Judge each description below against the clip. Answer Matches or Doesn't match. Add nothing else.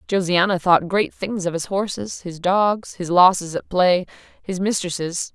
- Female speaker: Matches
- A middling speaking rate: Matches